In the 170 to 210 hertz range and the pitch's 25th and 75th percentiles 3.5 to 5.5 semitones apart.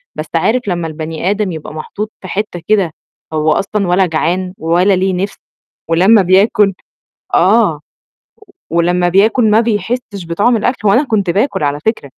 Yes: high, 190 Hz; average, 3.9 semitones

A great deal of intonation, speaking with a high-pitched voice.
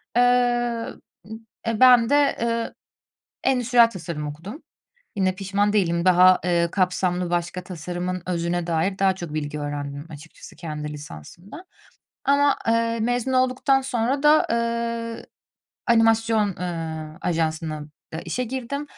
Yes: wide, 5.7 semitones; high, 195 Hz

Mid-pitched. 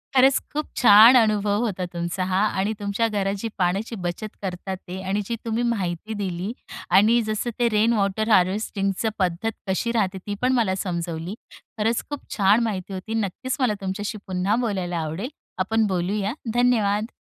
No: high, 205 Hz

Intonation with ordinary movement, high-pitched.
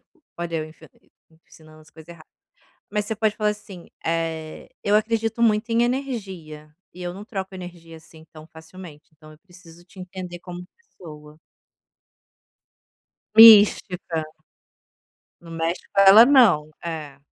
No: average, 4.6 semitones; medium, 175 Hz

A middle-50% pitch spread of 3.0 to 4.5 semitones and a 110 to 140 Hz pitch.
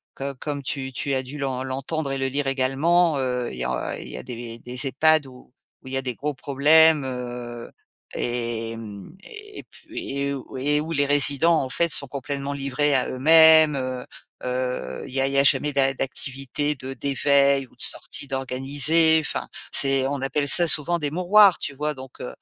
No: narrow, 2.4 semitones; low, 135 Hz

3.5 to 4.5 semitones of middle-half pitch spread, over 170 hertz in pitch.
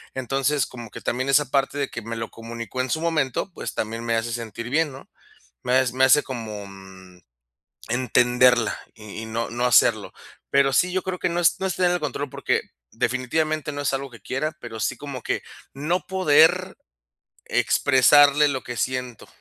No: average, 4.0 semitones; low, 130 Hz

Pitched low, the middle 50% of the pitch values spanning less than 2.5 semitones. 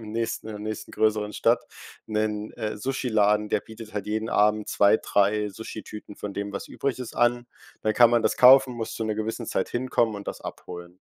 Yes: low, 110 Hz; narrow, 1.7 semitones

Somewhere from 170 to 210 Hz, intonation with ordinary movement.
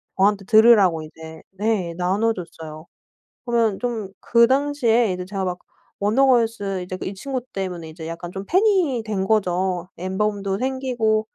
Yes: high, 200 Hz; average, 4.3 semitones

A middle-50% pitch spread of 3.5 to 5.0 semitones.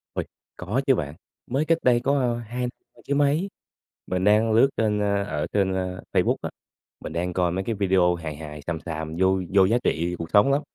No: wide, 5.4 semitones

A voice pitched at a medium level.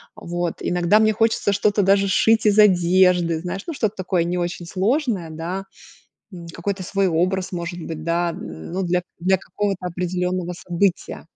Yes: medium, 180 Hz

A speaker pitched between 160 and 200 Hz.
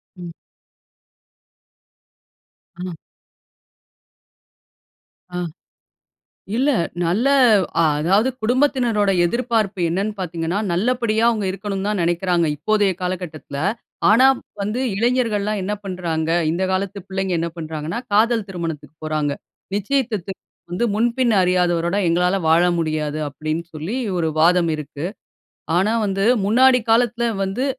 Yes: high, 190 Hz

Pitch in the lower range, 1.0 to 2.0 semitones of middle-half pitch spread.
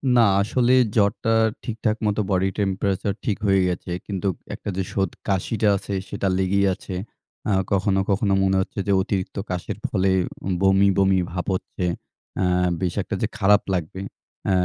Yes: very low, 95 Hz; narrow, 1.4 semitones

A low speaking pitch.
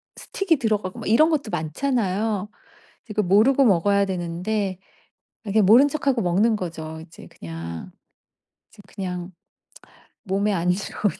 No: high, 200 Hz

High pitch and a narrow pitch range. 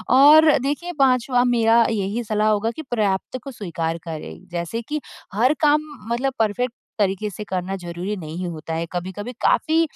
No: high, 215 Hz; wide, 5.6 semitones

